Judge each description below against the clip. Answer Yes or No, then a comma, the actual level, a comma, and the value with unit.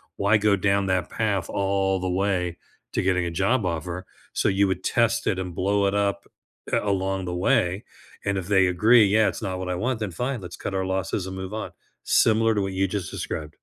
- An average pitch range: No, narrow, 1.8 semitones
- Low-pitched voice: Yes, very low, 95 Hz